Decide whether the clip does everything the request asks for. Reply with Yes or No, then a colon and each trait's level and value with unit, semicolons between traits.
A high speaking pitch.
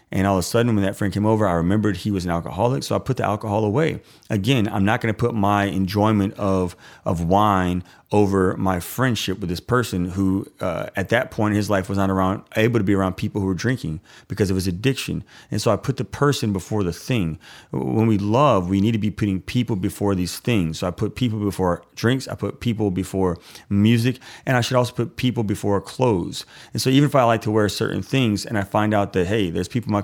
No: low, 105 Hz